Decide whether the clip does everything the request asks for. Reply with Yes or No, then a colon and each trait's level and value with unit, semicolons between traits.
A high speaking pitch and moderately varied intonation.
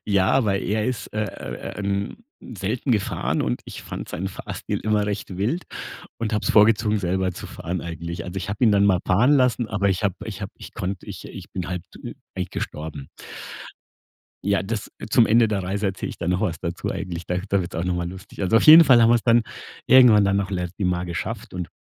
No: low, 100 Hz; average, 3.0 semitones